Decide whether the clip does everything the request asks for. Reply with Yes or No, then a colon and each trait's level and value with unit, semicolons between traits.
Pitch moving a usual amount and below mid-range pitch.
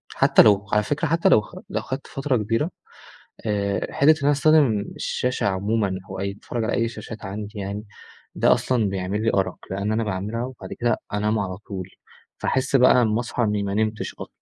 Yes: average, 3.4 semitones; low, 110 Hz